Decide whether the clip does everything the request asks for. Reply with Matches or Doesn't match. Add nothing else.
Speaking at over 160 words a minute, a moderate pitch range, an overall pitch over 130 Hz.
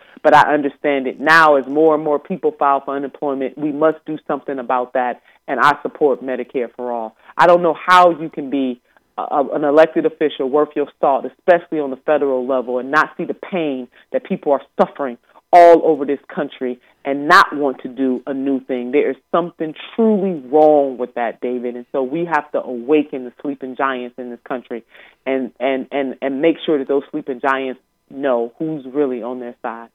Matches